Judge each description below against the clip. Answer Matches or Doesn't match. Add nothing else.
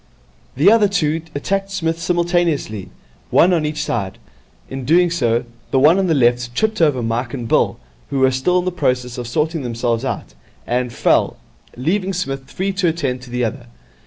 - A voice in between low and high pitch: Matches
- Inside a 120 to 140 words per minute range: Doesn't match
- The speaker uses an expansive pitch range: Matches